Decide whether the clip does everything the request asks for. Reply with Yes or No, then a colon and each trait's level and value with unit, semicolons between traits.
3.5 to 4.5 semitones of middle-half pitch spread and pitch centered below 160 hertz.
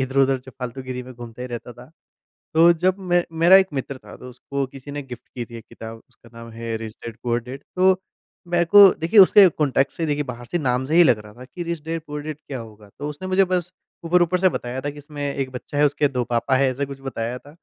No: average, 5.0 semitones; low, 135 Hz